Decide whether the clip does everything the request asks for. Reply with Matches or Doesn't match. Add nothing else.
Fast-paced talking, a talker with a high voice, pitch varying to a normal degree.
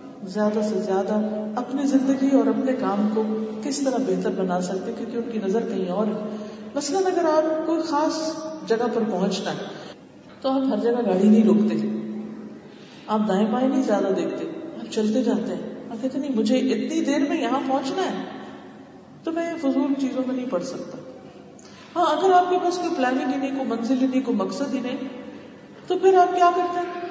Matches